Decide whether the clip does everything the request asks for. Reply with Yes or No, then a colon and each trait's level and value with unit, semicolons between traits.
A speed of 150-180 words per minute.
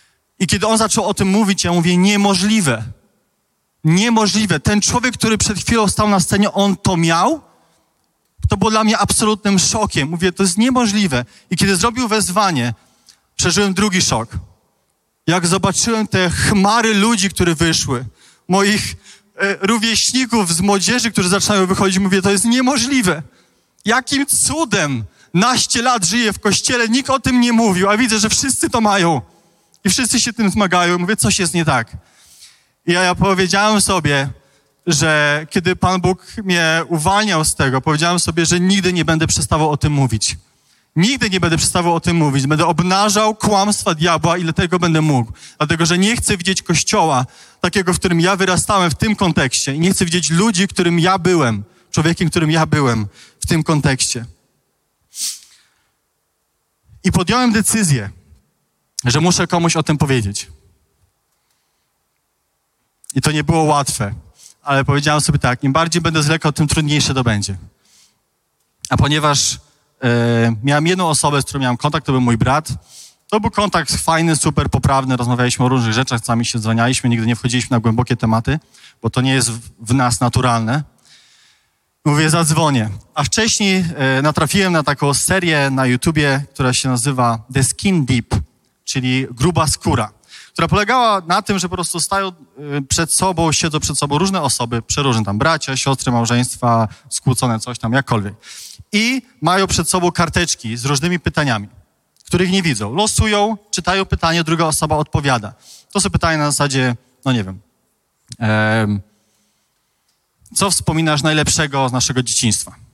Yes: average, 155 wpm